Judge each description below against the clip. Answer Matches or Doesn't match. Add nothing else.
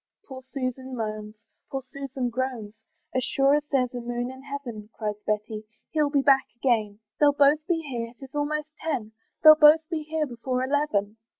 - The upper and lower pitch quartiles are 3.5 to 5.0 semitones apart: Matches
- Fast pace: Doesn't match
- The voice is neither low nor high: Doesn't match